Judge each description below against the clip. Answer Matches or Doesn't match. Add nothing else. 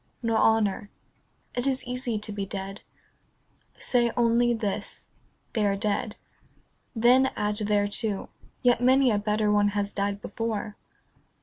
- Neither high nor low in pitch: Doesn't match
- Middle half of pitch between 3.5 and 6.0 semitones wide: Doesn't match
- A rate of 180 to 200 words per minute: Doesn't match